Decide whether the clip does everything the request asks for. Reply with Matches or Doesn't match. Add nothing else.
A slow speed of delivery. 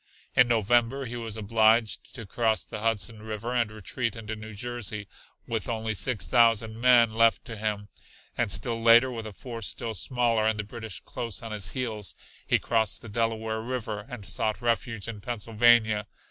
Doesn't match